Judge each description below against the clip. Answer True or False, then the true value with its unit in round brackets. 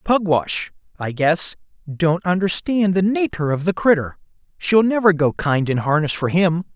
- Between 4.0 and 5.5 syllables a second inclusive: True (4.5 syllables/s)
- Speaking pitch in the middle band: True (175 Hz)